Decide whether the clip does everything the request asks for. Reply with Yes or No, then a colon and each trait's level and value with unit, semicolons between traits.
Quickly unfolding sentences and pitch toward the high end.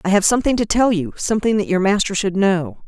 Yes: fast, 230 wpm; high, 195 Hz